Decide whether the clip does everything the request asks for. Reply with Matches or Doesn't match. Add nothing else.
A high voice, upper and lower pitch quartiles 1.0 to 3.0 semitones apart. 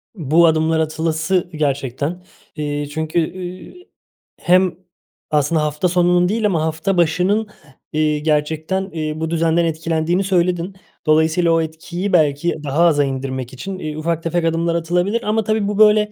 Doesn't match